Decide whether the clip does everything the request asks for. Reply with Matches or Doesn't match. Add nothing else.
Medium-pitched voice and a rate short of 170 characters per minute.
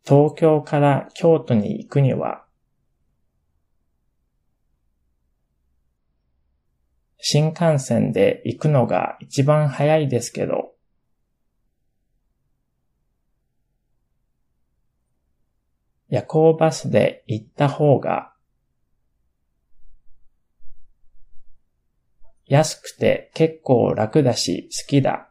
Doesn't match